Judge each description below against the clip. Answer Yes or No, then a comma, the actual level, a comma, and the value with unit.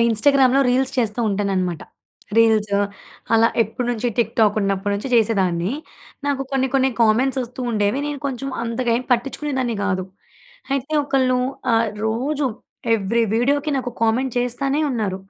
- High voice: Yes, high, 240 Hz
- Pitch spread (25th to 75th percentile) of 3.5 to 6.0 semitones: Yes, average, 3.8 semitones